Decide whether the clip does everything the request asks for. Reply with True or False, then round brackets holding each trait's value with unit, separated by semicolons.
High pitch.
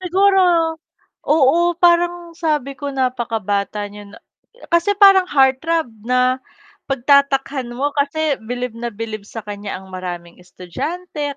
True (270 Hz)